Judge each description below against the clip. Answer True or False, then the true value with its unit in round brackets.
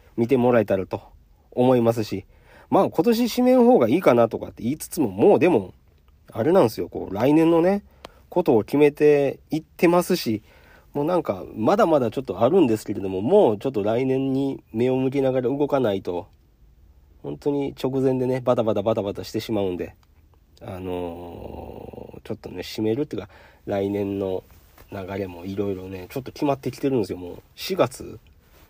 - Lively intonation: True (6.0 semitones)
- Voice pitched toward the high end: False (115 Hz)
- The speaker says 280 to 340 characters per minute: False (360 characters per minute)